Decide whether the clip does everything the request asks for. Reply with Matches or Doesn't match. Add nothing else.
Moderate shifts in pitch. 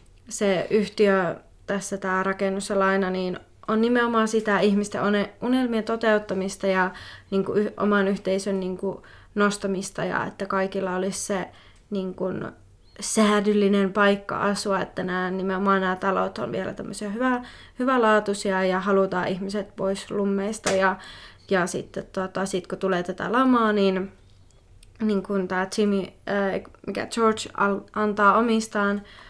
Doesn't match